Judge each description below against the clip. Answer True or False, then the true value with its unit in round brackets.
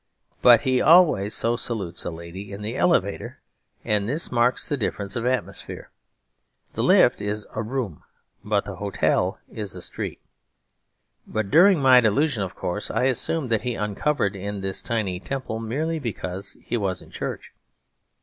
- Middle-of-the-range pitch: False (110 Hz)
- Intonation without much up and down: False (4.5 semitones)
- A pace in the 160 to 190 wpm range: True (165 wpm)